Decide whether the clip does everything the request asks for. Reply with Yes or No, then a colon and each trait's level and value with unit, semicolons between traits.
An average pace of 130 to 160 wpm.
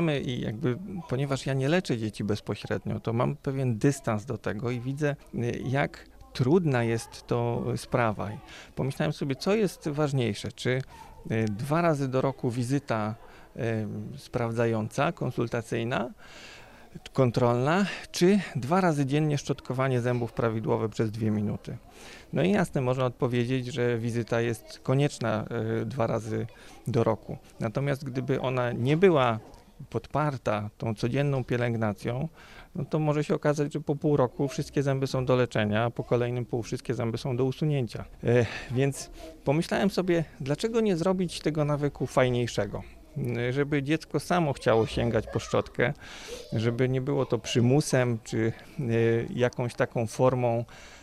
Yes: average, 135 wpm